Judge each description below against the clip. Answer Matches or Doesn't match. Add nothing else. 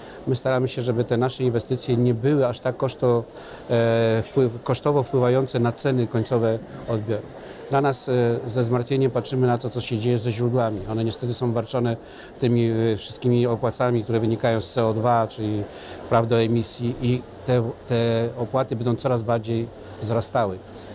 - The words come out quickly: Doesn't match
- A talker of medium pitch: Doesn't match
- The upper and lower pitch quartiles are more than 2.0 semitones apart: Doesn't match